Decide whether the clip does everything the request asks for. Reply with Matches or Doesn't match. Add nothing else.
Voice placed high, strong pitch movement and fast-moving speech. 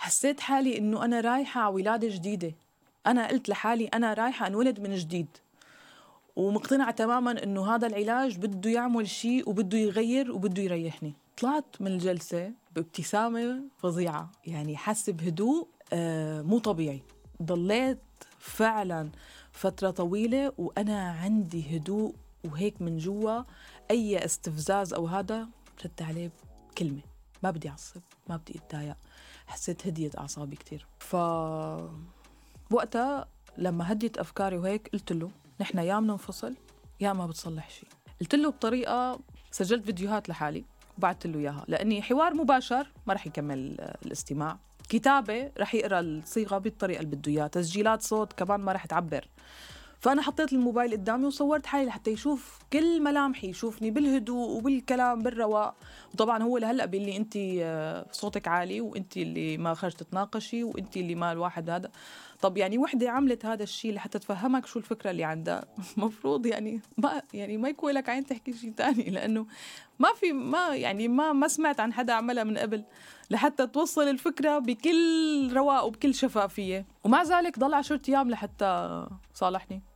Matches